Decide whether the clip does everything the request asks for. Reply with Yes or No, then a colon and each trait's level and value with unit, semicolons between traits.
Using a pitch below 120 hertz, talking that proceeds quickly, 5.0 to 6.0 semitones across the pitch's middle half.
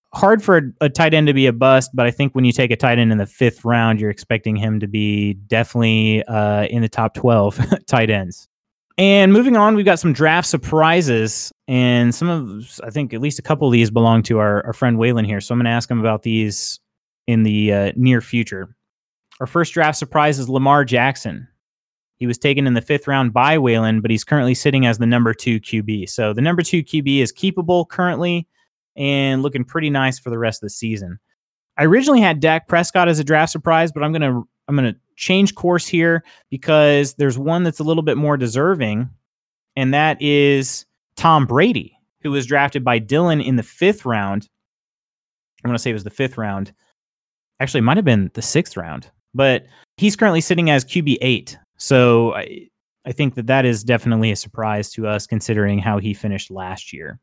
No: low, 125 Hz; fast, 210 wpm; average, 5.3 semitones